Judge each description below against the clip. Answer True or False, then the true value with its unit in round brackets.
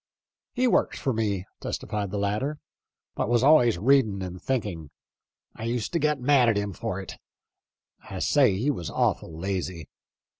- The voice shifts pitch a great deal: True (5.7 semitones)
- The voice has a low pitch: True (110 Hz)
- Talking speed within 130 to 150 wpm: False (175 wpm)